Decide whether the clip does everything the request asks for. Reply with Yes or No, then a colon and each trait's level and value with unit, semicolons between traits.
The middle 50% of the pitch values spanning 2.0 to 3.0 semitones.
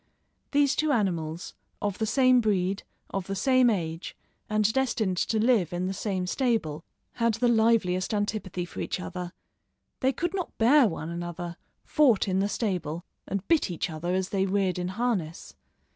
No: average, 4.6 semitones